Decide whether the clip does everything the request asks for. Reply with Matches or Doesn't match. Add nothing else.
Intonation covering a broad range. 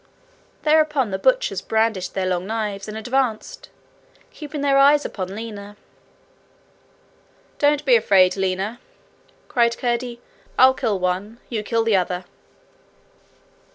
Doesn't match